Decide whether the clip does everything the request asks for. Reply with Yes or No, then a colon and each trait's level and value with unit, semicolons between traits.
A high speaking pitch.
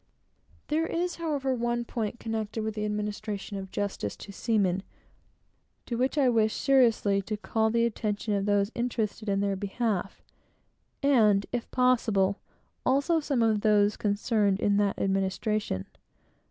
Yes: high, 215 Hz